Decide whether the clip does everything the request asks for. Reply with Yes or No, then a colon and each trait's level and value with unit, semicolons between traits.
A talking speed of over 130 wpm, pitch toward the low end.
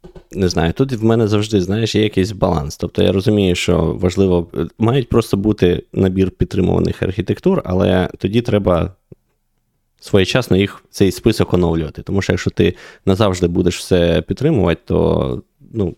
Yes: average, 145 wpm; very low, 95 Hz